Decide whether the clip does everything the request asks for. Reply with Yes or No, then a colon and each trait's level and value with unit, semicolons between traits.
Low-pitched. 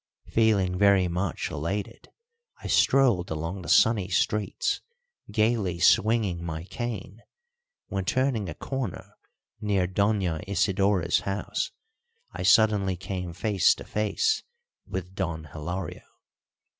Yes: very low, 95 Hz